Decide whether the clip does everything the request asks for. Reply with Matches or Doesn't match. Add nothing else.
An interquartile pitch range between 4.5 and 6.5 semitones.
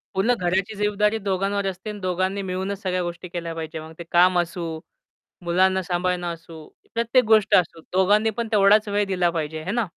Doesn't match